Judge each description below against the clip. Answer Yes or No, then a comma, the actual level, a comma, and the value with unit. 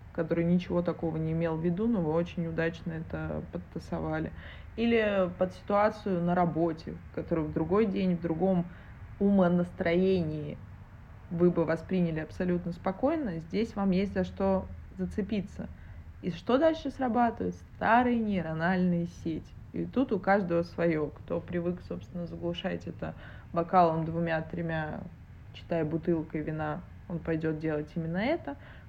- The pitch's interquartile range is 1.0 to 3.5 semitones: Yes, average, 3.0 semitones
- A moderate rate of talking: Yes, average, 130 wpm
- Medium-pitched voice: Yes, medium, 170 Hz